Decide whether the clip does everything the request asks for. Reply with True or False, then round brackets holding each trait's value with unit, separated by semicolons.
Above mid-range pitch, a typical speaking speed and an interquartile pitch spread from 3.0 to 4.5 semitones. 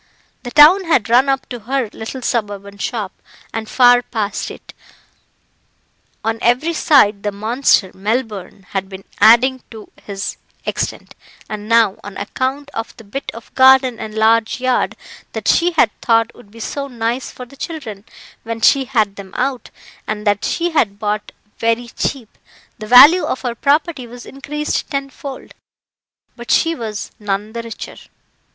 True (235 Hz; 160 wpm; 3.9 semitones)